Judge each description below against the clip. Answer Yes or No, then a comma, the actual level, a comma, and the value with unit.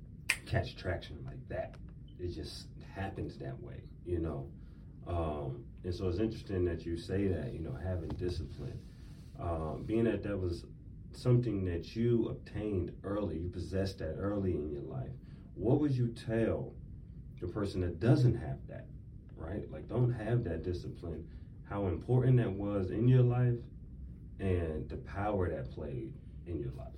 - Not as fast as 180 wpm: Yes, average, 160 wpm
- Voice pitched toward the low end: Yes, very low, 95 Hz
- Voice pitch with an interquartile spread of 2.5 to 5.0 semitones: No, wide, 5.4 semitones